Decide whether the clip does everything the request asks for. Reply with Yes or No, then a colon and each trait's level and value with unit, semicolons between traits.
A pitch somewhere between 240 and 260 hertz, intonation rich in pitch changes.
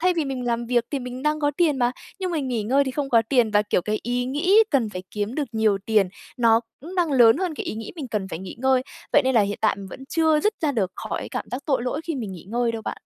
No: very high, 250 Hz; average, 4.8 semitones